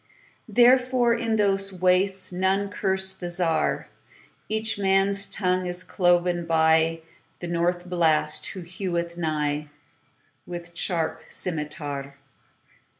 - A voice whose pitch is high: No, medium, 180 Hz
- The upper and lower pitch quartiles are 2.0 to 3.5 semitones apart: Yes, average, 2.8 semitones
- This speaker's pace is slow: Yes, slow, 90 wpm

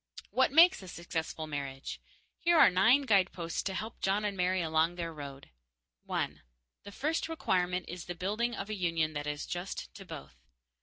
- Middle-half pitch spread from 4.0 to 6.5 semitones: Yes, average, 4.5 semitones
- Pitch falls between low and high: Yes, medium, 180 Hz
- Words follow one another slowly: No, average, 175 wpm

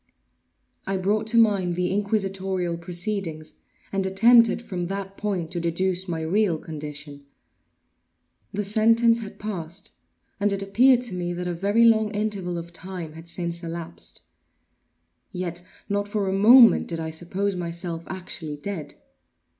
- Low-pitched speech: No, high, 190 Hz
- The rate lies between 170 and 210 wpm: No, average, 145 wpm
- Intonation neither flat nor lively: Yes, average, 3.2 semitones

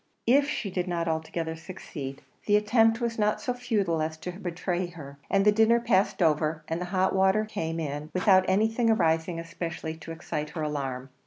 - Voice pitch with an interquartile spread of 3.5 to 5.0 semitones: Yes, average, 4.6 semitones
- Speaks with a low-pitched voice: No, medium, 175 Hz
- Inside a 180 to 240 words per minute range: Yes, average, 185 wpm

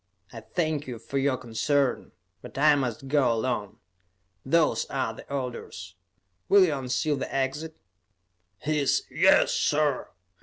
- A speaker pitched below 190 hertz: Yes, low, 135 Hz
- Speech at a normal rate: No, slow, 130 wpm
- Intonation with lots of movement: No, average, 3.1 semitones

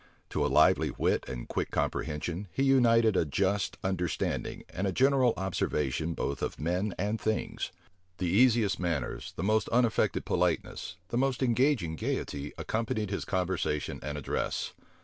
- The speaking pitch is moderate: No, very low, 95 Hz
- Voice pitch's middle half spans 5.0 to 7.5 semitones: Yes, wide, 5.5 semitones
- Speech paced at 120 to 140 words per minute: No, average, 150 wpm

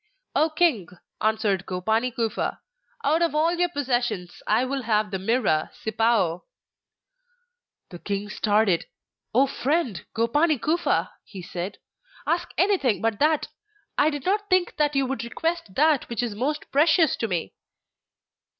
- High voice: Yes, high, 245 Hz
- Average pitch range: No, wide, 6.7 semitones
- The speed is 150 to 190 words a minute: No, average, 140 wpm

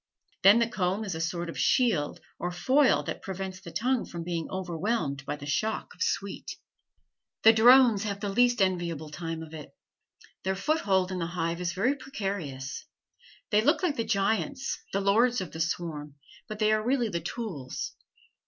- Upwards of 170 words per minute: Yes, average, 180 wpm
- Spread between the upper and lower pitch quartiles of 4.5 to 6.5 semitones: Yes, average, 5.0 semitones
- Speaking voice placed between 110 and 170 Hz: No, high, 190 Hz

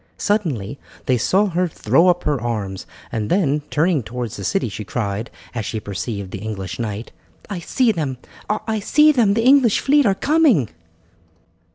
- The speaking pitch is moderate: Yes, medium, 145 Hz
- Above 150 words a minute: Yes, average, 170 wpm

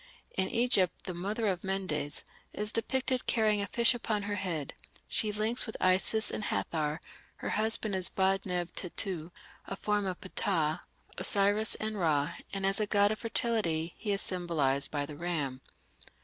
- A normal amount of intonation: Yes, average, 3.9 semitones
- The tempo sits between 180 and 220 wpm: No, average, 165 wpm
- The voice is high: Yes, high, 195 Hz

